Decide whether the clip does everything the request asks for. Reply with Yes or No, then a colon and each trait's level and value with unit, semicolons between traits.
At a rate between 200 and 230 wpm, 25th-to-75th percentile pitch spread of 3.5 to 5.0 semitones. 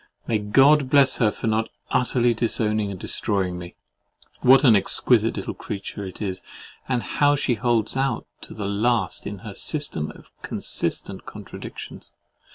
No: average, 155 wpm; average, 4.3 semitones